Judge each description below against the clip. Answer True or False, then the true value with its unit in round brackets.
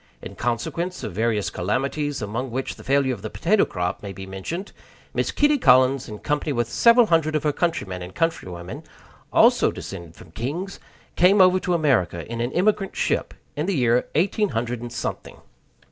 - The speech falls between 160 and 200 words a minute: True (180 wpm)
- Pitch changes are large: True (8.1 semitones)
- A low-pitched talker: True (130 Hz)